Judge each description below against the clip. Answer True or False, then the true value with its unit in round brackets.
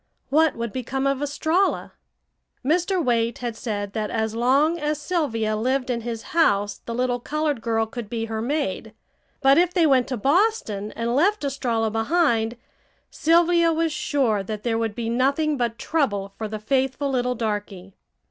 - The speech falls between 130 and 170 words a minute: True (165 wpm)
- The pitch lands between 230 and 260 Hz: True (250 Hz)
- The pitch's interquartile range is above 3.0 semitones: True (5.1 semitones)